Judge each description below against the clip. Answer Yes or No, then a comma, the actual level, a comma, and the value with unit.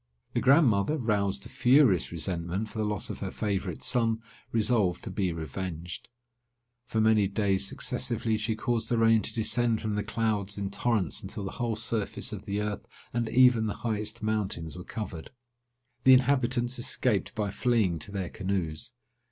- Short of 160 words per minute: No, average, 170 wpm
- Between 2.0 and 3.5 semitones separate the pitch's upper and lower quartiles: Yes, average, 3.1 semitones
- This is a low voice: Yes, low, 105 Hz